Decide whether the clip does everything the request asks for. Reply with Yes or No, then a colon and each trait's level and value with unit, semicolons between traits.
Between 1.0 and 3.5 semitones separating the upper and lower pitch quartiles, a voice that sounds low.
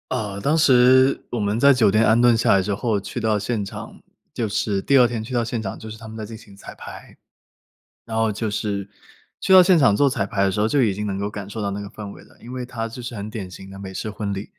Yes: average, 3.2 semitones; low, 110 Hz